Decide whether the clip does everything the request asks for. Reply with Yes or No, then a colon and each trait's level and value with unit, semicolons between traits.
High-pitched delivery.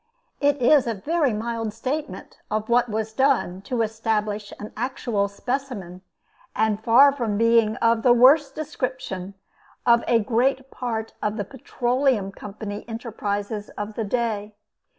Yes: high, 230 Hz